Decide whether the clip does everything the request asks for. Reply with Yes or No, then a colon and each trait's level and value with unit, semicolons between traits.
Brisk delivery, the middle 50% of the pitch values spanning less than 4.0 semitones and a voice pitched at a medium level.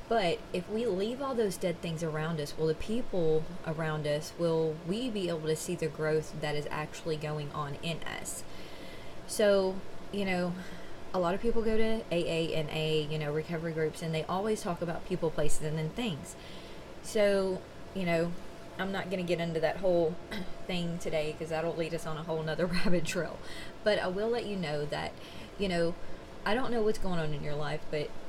Yes: fast, 210 wpm; average, 3.3 semitones; medium, 170 Hz